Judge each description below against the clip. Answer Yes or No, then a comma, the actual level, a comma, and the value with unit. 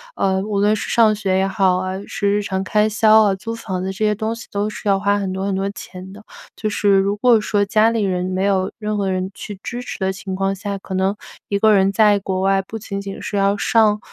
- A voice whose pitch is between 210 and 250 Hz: No, high, 200 Hz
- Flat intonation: Yes, narrow, 1.7 semitones